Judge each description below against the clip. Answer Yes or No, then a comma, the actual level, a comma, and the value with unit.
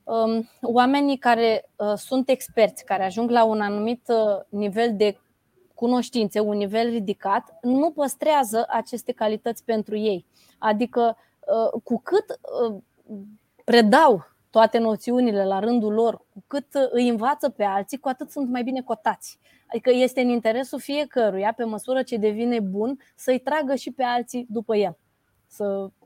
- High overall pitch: Yes, high, 235 Hz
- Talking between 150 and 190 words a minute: No, average, 140 wpm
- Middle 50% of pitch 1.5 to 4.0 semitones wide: Yes, average, 3.1 semitones